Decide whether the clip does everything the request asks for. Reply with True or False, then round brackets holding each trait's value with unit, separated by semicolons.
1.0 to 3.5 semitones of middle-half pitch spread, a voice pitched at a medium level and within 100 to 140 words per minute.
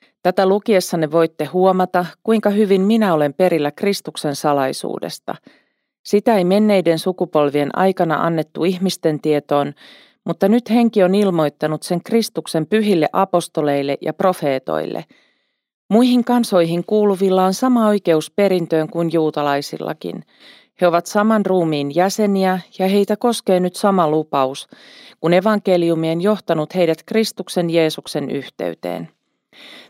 False (4.6 semitones; 180 Hz; 115 wpm)